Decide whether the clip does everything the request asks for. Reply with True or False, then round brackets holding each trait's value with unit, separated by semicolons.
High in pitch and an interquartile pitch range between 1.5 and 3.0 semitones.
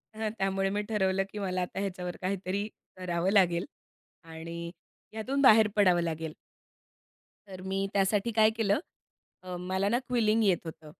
True (195 Hz; 2.6 semitones)